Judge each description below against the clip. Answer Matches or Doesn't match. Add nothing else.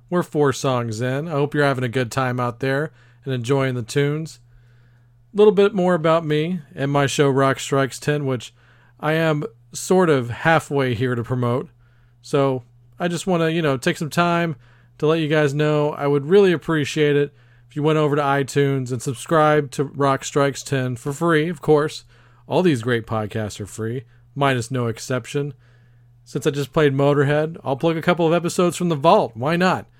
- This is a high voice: Doesn't match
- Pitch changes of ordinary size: Matches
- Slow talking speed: Doesn't match